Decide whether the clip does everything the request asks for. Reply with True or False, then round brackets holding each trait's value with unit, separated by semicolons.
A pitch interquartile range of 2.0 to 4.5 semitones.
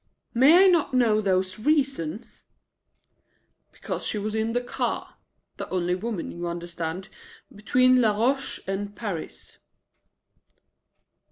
False (5.3 semitones)